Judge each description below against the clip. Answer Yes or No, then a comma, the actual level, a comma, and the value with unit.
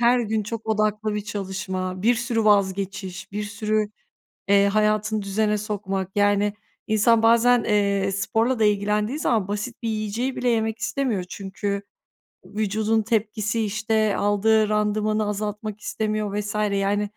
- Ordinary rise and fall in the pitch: No, narrow, 1.5 semitones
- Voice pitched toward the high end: Yes, high, 210 Hz